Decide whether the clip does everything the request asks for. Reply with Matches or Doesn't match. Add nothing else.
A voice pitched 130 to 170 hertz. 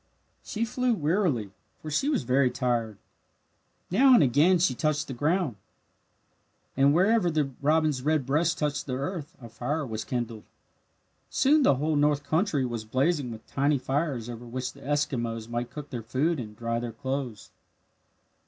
Matches